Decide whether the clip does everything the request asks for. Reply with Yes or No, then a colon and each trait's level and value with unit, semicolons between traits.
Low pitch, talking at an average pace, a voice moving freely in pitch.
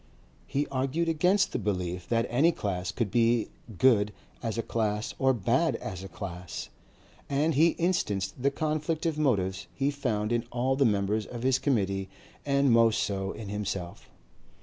Yes: low, 115 Hz; average, 165 wpm; wide, 5.7 semitones